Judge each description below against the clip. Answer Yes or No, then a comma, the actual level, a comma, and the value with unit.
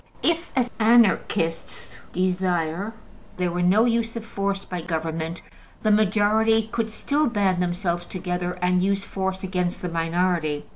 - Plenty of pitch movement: No, average, 3.6 semitones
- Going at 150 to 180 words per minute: No, average, 140 wpm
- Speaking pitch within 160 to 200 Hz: Yes, medium, 185 Hz